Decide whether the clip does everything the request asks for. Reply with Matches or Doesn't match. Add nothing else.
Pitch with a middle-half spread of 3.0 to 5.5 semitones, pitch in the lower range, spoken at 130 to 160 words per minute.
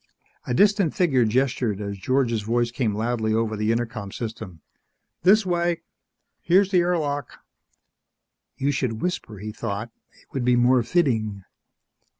Matches